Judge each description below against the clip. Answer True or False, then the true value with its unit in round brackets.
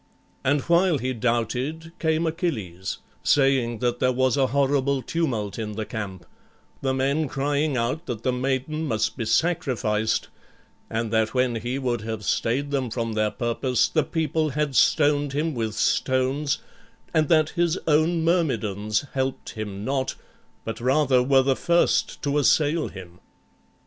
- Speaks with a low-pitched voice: True (130 Hz)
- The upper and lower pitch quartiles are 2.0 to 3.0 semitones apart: False (4.7 semitones)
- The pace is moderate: True (150 wpm)